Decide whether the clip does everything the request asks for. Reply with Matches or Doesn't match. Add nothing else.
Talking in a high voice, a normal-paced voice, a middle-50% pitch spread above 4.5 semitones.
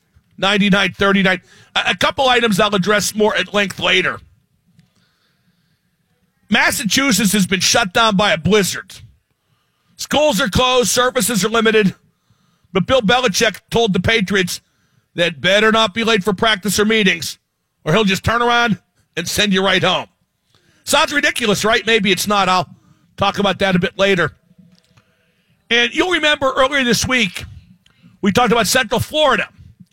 Doesn't match